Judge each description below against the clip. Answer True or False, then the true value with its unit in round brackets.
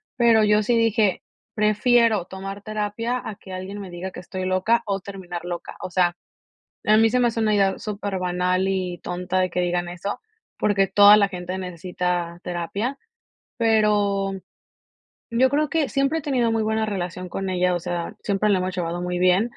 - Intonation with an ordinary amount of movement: True (3.2 semitones)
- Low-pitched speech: False (195 Hz)